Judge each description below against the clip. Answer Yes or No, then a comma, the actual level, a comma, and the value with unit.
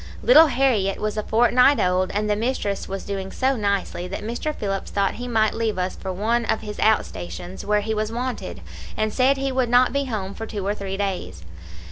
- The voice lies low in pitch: No, high, 215 Hz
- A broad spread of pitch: No, average, 3.7 semitones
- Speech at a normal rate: No, fast, 215 wpm